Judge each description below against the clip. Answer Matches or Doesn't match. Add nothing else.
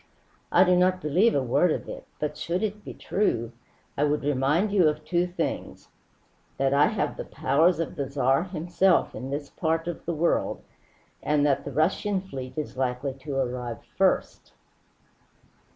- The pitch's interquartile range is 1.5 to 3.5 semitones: Doesn't match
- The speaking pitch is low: Doesn't match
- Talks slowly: Doesn't match